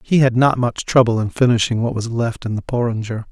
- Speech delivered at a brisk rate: Yes, fast, 235 wpm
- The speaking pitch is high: No, low, 120 Hz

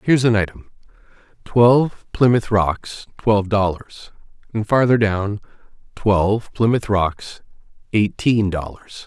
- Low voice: Yes, low, 105 Hz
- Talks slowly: Yes, slow, 105 wpm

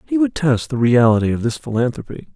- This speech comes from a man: Yes, male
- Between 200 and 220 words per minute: Yes, fast, 205 wpm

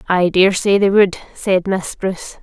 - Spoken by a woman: Yes, female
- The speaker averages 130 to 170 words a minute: No, average, 200 wpm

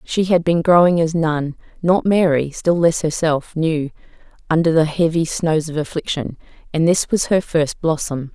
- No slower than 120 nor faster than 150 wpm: No, average, 175 wpm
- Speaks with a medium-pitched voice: Yes, medium, 160 Hz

